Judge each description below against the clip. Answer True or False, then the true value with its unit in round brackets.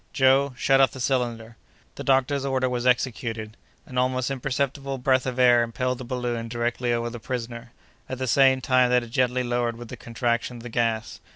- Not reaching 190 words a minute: False (195 wpm)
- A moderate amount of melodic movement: False (1.8 semitones)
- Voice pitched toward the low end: True (125 Hz)